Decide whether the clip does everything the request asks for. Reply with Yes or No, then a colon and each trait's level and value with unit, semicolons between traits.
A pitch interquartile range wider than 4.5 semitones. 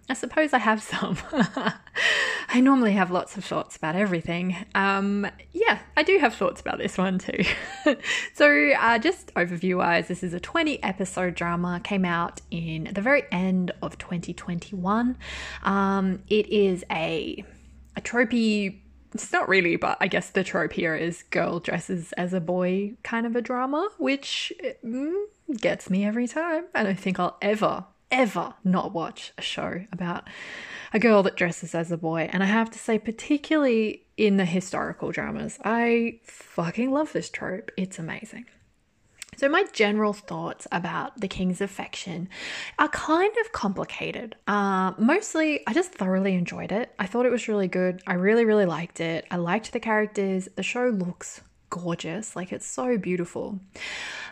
Yes: wide, 5.6 semitones